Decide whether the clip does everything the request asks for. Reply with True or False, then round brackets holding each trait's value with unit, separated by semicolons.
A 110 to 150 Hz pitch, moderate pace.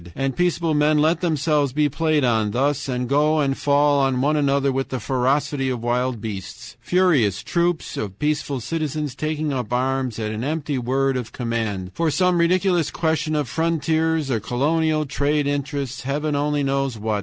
True (140 Hz; 175 wpm)